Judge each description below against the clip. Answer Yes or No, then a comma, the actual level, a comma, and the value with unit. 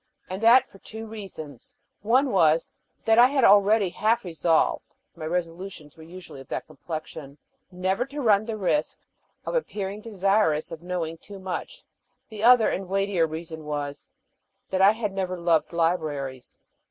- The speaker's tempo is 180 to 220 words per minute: No, average, 155 wpm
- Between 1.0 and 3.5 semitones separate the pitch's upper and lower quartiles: No, average, 4.9 semitones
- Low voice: No, medium, 185 Hz